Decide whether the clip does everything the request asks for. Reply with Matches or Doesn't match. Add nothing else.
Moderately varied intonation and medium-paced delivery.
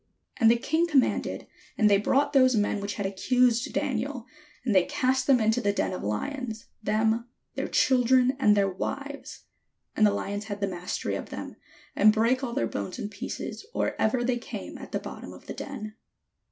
Matches